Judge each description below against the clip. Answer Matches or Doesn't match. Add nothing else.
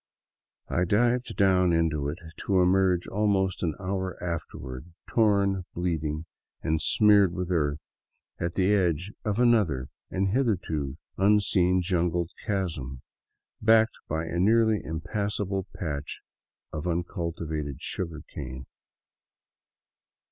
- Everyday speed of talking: Doesn't match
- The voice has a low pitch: Matches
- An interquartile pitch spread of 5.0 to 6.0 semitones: Doesn't match